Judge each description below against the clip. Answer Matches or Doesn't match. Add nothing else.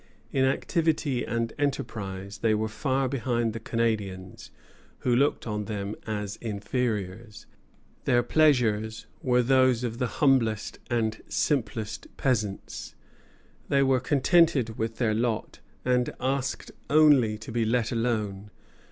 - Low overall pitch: Matches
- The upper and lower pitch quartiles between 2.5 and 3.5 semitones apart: Matches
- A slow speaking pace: Matches